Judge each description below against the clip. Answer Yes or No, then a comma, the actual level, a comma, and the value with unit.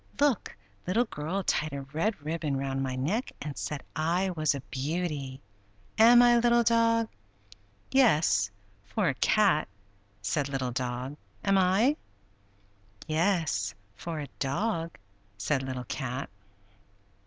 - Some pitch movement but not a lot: No, wide, 7.1 semitones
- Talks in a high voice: No, medium, 155 Hz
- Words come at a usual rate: No, slow, 125 wpm